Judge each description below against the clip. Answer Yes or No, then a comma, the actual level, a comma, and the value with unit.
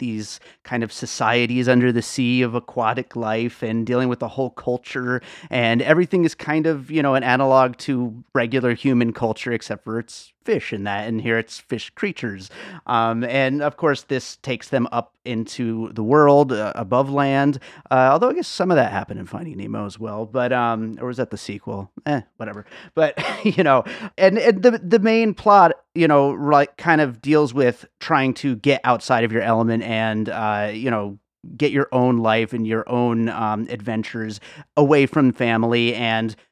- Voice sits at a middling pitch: No, low, 125 Hz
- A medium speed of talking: Yes, average, 190 wpm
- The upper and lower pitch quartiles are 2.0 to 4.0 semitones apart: Yes, average, 3.7 semitones